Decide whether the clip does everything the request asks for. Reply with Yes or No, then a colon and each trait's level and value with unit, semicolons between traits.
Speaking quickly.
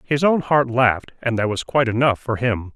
Yes: fast, 240 wpm